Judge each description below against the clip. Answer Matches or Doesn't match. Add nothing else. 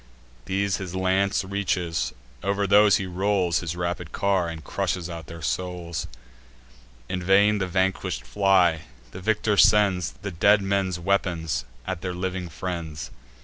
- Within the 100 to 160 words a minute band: Matches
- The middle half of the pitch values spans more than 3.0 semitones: Doesn't match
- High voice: Doesn't match